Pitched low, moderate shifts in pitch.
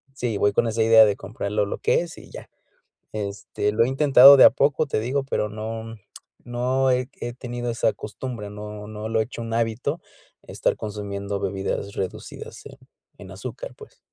Yes: low, 115 Hz; average, 3.1 semitones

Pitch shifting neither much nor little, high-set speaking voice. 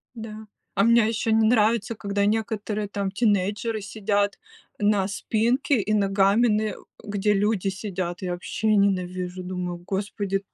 No: narrow, 2.0 semitones; high, 205 Hz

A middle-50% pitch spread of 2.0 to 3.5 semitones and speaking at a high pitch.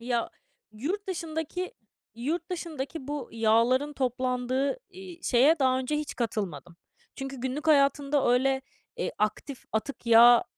No: average, 3.9 semitones; very high, 270 Hz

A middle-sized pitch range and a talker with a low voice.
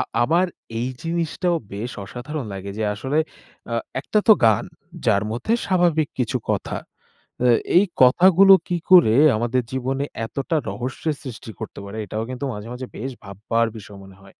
No: wide, 6.8 semitones; low, 125 Hz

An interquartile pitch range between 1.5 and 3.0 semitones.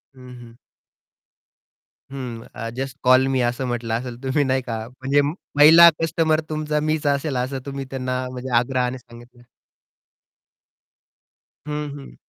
Yes: average, 2.7 semitones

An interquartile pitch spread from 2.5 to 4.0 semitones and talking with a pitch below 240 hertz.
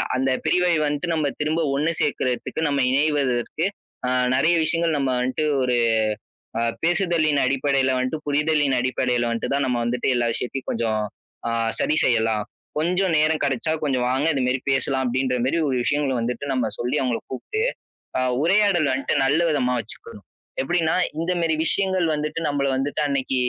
Yes: average, 3.7 semitones; medium, 140 Hz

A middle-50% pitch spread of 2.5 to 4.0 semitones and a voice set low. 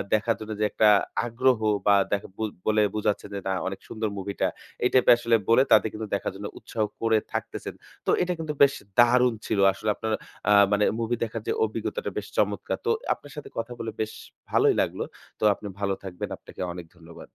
Yes: average, 2.8 semitones; low, 110 Hz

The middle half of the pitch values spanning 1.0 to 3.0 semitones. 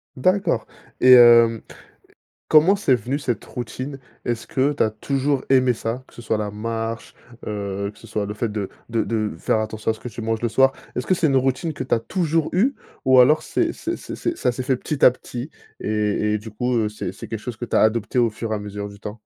No: average, 3.6 semitones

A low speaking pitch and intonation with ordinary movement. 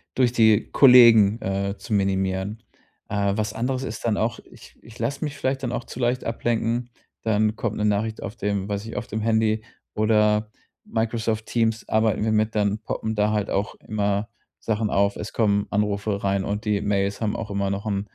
No: low, 110 Hz; narrow, 2.0 semitones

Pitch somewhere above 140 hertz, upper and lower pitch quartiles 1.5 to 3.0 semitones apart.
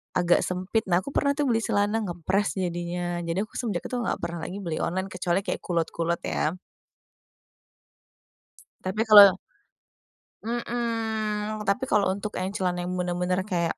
No: high, 190 Hz; average, 3.6 semitones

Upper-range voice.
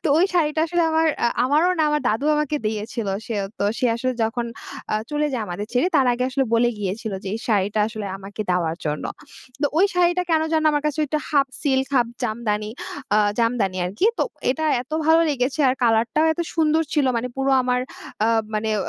Yes: very high, 250 Hz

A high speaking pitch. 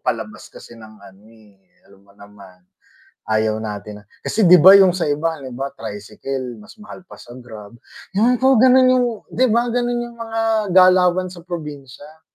No: medium, 145 Hz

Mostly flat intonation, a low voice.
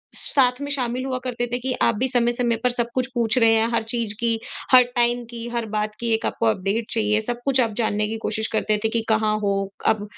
No: narrow, 2.0 semitones; high, 235 Hz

